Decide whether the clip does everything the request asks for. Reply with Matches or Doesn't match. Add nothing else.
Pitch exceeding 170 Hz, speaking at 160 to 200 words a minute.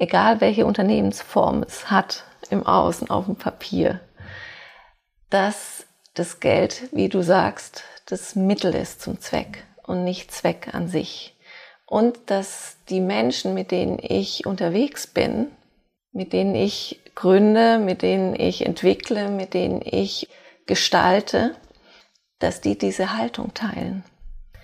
Doesn't match